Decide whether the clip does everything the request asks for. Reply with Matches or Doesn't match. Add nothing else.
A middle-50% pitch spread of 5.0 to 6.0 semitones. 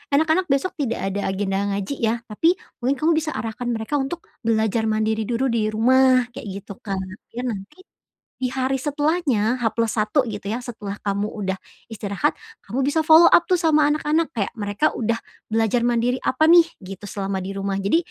Matches